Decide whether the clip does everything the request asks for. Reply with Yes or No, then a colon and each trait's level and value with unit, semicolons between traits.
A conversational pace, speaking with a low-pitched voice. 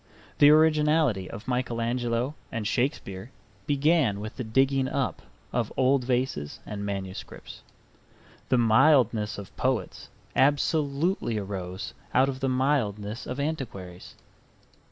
No: slow, 115 wpm; low, 125 Hz